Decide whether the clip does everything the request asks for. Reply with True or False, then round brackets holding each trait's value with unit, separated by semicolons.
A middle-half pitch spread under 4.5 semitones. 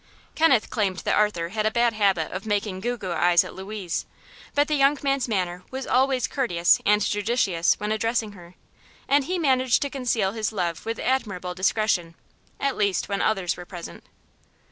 False (5.1 semitones)